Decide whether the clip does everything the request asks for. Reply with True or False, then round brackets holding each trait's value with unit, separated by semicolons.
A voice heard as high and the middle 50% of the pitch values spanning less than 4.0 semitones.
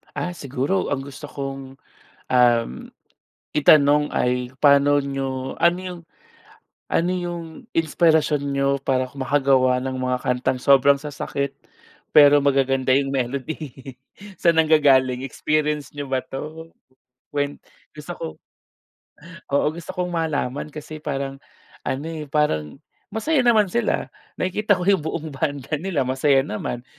False (140 Hz; 3.0 semitones)